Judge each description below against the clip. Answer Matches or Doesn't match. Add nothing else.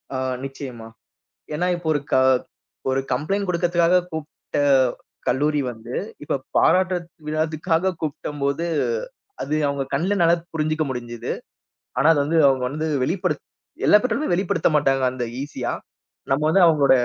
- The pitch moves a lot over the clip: Doesn't match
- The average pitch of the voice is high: Doesn't match